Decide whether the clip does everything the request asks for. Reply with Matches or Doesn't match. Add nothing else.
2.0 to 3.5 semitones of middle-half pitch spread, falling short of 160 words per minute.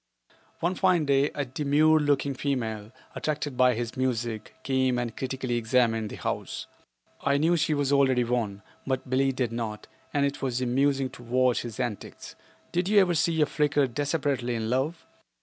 Doesn't match